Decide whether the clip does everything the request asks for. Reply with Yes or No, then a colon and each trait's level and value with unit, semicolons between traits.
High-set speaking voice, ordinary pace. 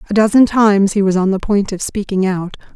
No: high, 200 Hz; fast, 240 wpm